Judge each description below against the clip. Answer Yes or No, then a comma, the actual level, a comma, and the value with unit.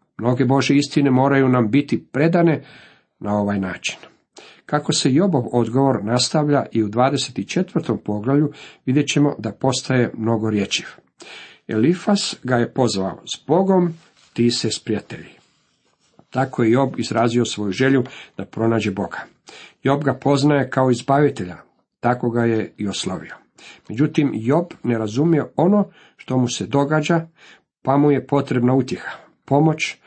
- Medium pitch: No, low, 130 Hz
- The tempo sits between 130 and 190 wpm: Yes, average, 135 wpm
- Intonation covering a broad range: No, average, 4.0 semitones